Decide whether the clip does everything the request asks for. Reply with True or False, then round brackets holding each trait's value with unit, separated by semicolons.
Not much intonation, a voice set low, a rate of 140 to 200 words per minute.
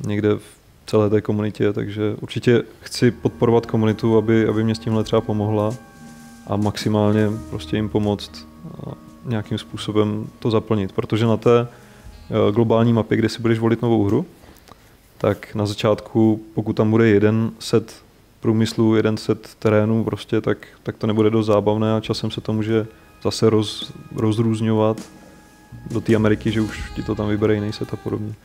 True (1.2 semitones; 110 Hz; 160 wpm)